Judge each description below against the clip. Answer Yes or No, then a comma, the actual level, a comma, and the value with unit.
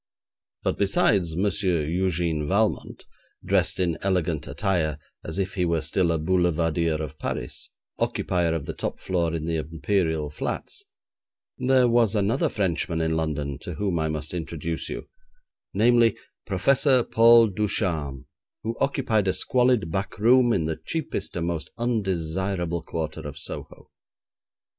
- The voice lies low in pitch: Yes, very low, 85 Hz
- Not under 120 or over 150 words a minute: Yes, average, 140 wpm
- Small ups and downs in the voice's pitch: No, average, 4.2 semitones